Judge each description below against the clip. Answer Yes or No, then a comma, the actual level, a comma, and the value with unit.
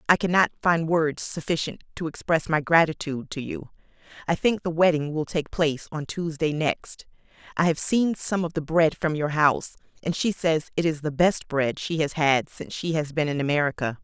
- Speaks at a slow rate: No, fast, 205 wpm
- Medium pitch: Yes, medium, 160 Hz